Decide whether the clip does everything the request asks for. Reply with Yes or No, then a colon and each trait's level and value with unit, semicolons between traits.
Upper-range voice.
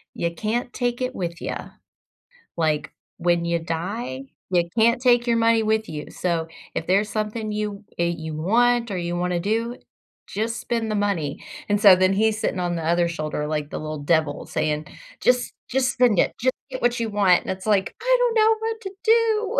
Yes: high, 205 Hz